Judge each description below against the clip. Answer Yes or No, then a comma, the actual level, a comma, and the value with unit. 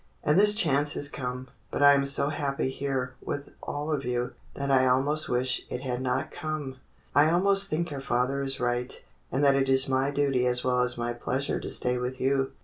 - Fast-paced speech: Yes, fast, 215 wpm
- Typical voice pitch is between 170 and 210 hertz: No, low, 135 Hz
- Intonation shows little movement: Yes, narrow, 2.2 semitones